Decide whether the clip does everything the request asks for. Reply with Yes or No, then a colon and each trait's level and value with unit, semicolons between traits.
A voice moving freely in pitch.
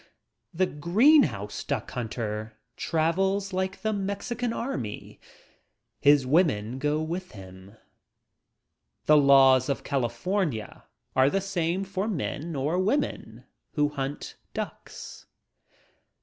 Yes: wide, 6.7 semitones